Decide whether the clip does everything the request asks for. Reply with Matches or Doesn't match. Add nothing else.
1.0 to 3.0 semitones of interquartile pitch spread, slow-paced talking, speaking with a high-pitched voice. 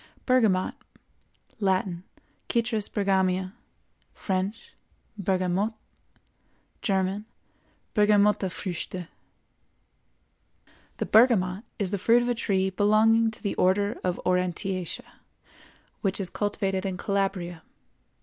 Matches